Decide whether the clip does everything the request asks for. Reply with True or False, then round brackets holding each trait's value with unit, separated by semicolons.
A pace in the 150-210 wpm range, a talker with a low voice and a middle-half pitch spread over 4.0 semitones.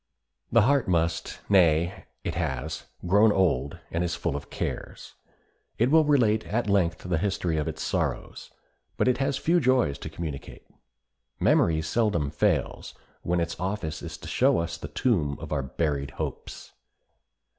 True (155 wpm; 85 Hz; 5.4 semitones)